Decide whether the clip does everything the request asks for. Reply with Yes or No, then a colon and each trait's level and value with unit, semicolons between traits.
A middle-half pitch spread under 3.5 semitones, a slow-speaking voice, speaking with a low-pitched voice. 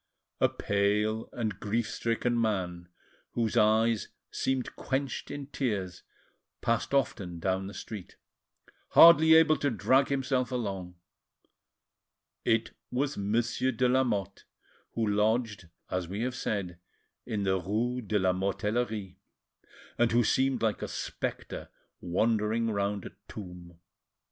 No: average, 3.8 semitones; slow, 125 wpm; low, 110 Hz